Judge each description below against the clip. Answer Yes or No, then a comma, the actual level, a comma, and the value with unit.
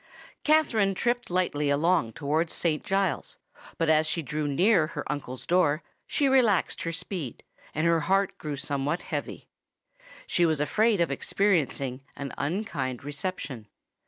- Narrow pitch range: No, average, 4.9 semitones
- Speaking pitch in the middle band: Yes, medium, 160 Hz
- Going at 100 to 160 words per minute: Yes, average, 140 wpm